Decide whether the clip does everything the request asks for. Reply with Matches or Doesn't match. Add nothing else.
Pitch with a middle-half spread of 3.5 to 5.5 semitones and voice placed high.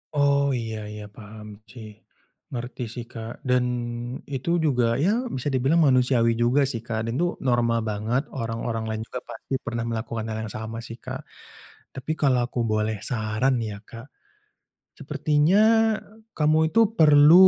Doesn't match